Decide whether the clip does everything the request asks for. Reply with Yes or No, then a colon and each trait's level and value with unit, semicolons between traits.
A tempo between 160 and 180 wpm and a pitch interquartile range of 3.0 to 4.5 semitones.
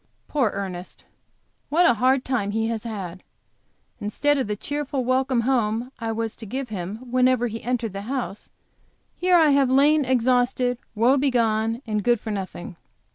Yes: average, 165 wpm; average, 3.4 semitones